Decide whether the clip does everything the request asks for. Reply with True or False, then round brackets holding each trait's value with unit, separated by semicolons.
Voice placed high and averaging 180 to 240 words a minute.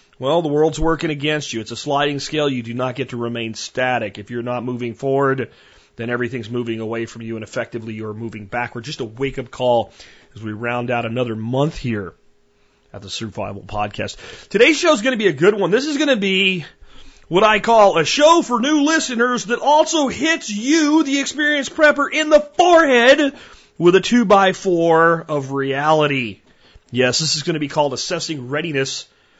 False (145 Hz; 200 wpm)